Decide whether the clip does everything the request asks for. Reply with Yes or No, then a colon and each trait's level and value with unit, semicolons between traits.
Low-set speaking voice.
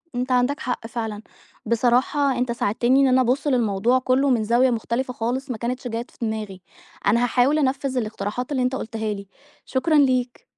No: high, 245 Hz